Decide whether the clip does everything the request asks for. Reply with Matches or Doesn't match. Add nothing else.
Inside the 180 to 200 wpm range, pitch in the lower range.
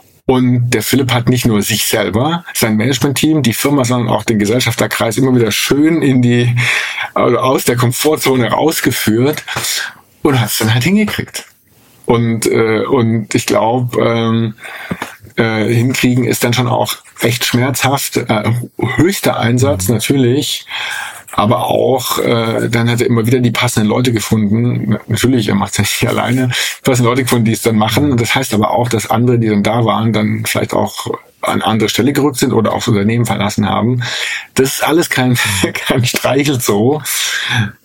Doesn't match